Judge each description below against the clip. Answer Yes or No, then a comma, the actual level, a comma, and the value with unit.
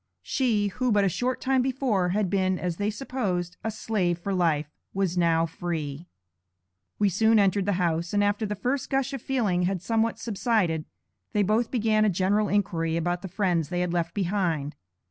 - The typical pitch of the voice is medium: No, high, 195 Hz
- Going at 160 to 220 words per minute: Yes, average, 185 wpm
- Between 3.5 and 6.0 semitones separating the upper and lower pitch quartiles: Yes, average, 3.8 semitones